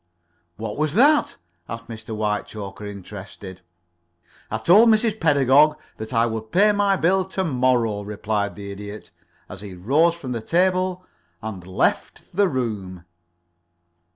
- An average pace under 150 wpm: Yes, slow, 135 wpm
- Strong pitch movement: Yes, wide, 8.9 semitones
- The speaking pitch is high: No, low, 115 Hz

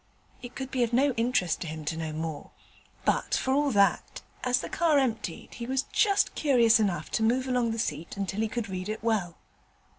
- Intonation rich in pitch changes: Yes, wide, 5.7 semitones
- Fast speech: Yes, fast, 210 wpm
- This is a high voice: Yes, high, 225 Hz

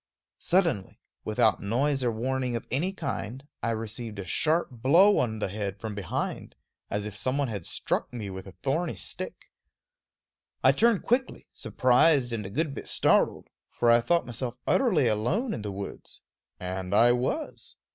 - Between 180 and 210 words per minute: No, average, 165 wpm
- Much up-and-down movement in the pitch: Yes, wide, 5.8 semitones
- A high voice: No, low, 120 Hz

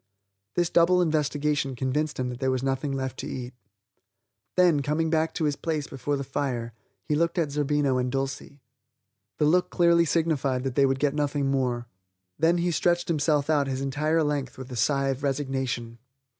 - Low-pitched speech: No, medium, 145 Hz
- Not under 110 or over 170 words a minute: No, average, 185 wpm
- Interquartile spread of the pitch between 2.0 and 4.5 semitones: Yes, average, 2.9 semitones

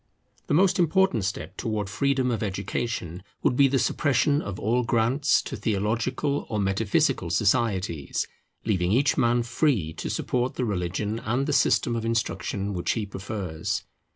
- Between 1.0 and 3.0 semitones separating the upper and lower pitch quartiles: No, average, 4.7 semitones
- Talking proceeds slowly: No, average, 155 wpm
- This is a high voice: No, low, 115 Hz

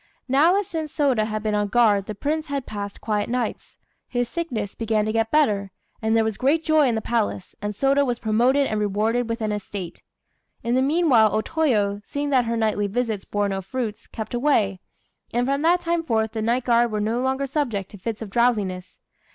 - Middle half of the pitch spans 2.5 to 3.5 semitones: No, average, 4.4 semitones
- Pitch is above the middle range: Yes, high, 230 Hz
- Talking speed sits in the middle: No, fast, 210 wpm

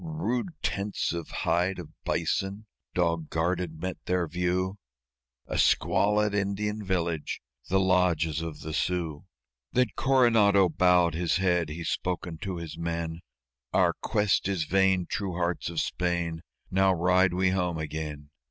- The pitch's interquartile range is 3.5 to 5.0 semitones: No, narrow, 2.6 semitones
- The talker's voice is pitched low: Yes, very low, 90 Hz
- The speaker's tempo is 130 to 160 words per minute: Yes, average, 140 wpm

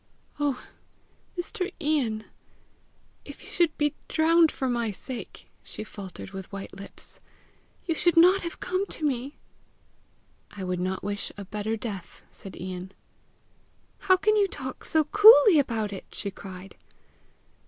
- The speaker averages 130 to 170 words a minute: Yes, average, 145 wpm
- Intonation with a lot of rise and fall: Yes, wide, 9.0 semitones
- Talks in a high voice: Yes, very high, 255 Hz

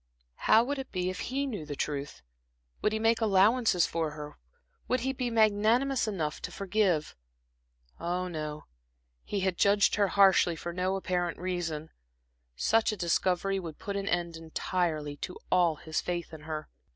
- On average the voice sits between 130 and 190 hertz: Yes, medium, 185 Hz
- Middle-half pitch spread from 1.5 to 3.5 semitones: No, average, 4.6 semitones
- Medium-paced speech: Yes, average, 165 wpm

